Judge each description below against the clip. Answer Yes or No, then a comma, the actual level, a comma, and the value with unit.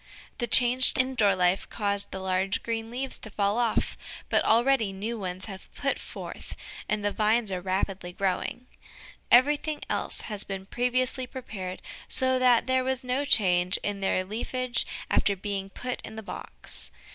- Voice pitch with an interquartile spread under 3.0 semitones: No, average, 4.5 semitones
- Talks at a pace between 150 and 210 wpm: Yes, average, 165 wpm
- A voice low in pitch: No, high, 220 Hz